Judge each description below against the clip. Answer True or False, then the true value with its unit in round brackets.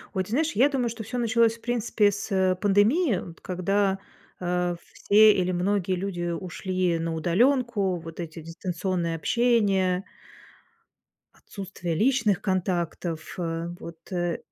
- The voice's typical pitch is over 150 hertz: True (190 Hz)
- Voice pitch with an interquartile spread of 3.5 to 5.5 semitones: True (3.8 semitones)